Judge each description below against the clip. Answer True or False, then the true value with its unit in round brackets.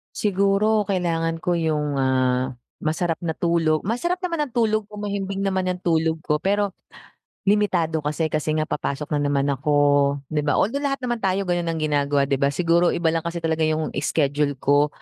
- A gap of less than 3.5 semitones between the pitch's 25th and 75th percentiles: False (4.8 semitones)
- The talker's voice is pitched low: False (165 Hz)